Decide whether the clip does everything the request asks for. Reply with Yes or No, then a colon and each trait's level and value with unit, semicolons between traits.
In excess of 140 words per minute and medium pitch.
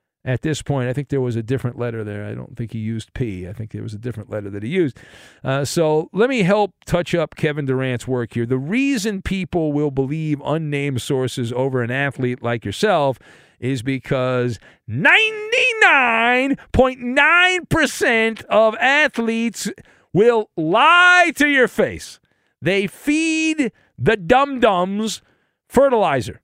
Yes: average, 150 wpm; medium, 155 Hz